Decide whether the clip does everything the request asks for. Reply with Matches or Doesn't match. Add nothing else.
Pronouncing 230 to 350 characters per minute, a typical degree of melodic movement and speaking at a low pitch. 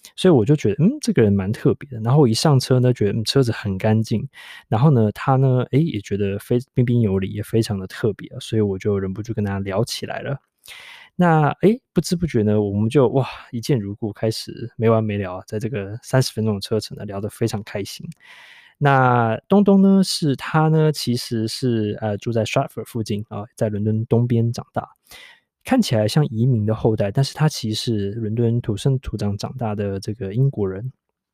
Matches